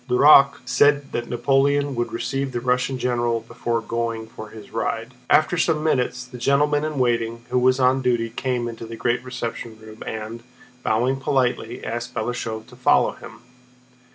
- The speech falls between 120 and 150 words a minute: No, average, 165 wpm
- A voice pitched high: No, low, 125 Hz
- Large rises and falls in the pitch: No, narrow, 2.5 semitones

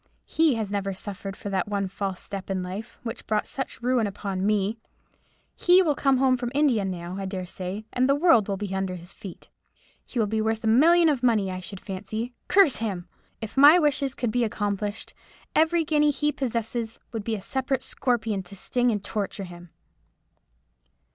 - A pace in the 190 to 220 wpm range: Yes, average, 195 wpm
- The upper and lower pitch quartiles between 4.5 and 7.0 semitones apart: Yes, average, 4.9 semitones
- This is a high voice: Yes, high, 220 Hz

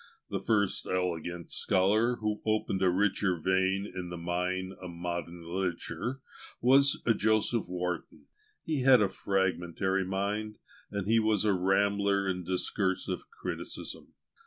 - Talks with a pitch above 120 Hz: No, very low, 95 Hz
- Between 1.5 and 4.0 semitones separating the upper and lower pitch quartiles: Yes, average, 2.8 semitones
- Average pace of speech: No, slow, 130 wpm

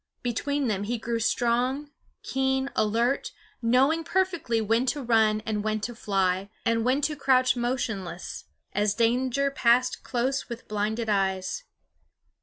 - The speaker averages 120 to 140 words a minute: Yes, slow, 135 wpm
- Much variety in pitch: No, average, 3.6 semitones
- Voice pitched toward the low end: No, high, 235 Hz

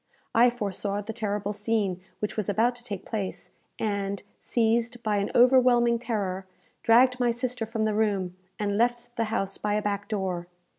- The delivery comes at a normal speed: Yes, average, 170 wpm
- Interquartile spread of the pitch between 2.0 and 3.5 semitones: Yes, average, 2.8 semitones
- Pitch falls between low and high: No, high, 215 Hz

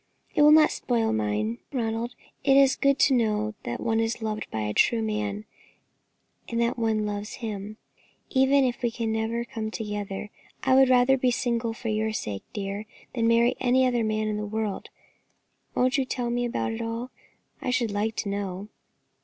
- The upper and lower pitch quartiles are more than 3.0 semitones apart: No, narrow, 2.6 semitones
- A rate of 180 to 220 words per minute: Yes, average, 185 wpm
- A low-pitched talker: No, high, 225 Hz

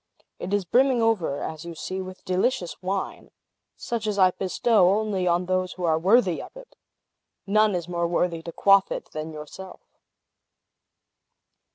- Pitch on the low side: No, medium, 185 Hz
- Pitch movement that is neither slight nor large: Yes, average, 3.1 semitones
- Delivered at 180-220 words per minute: No, average, 160 wpm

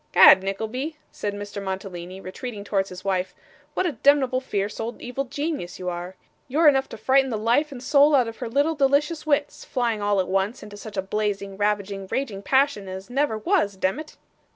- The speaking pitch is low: No, high, 220 Hz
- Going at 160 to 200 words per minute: Yes, average, 195 wpm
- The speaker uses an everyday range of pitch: No, wide, 5.8 semitones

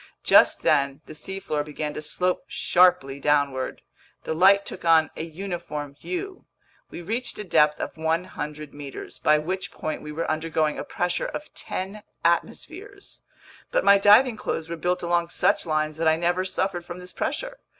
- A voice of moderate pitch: Yes, medium, 170 Hz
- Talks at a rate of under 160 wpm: No, average, 170 wpm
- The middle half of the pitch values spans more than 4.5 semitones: No, average, 4.0 semitones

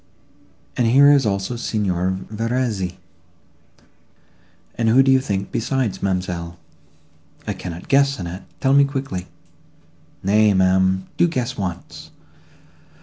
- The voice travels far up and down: Yes, wide, 5.7 semitones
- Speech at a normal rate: No, slow, 115 wpm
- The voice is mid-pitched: No, low, 105 Hz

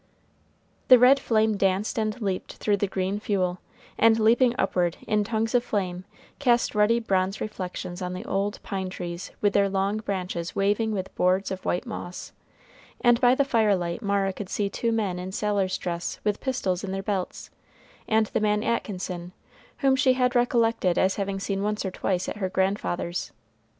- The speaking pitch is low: No, high, 200 Hz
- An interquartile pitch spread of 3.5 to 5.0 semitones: No, average, 3.0 semitones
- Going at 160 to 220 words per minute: Yes, average, 175 wpm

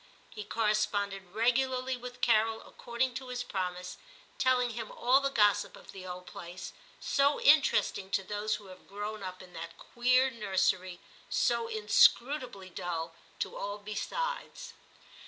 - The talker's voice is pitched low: No, high, 215 Hz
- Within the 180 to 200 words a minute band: No, average, 145 wpm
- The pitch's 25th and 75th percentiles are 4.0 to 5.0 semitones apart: Yes, average, 4.7 semitones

